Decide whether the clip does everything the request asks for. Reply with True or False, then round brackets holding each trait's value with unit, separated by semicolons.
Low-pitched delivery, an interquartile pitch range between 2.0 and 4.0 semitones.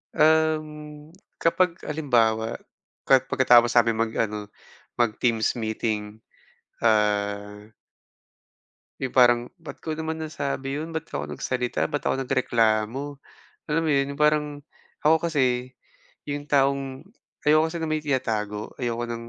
False (130 Hz; 5.1 semitones)